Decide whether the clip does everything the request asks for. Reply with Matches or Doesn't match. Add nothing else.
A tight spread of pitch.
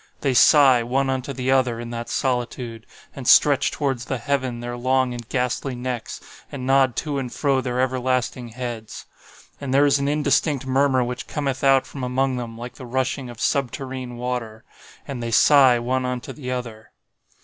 Matches